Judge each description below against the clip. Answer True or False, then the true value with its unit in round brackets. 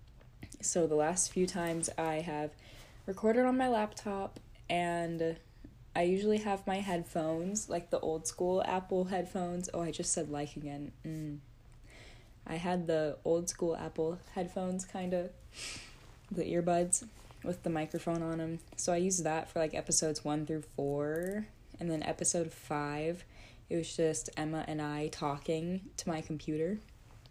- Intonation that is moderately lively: True (3.0 semitones)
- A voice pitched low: False (165 Hz)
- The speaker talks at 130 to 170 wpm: True (155 wpm)